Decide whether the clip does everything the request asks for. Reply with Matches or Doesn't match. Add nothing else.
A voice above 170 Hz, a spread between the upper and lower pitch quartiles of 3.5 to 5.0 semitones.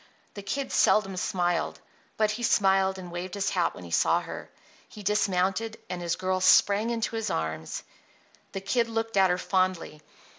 Doesn't match